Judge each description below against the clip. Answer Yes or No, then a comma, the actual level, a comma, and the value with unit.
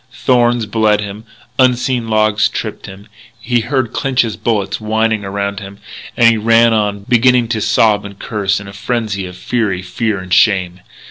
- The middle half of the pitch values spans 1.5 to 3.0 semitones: Yes, average, 2.7 semitones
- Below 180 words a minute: Yes, average, 170 wpm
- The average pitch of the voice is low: Yes, low, 110 Hz